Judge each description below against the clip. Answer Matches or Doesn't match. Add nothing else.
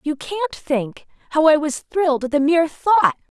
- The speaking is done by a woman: Matches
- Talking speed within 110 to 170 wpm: Doesn't match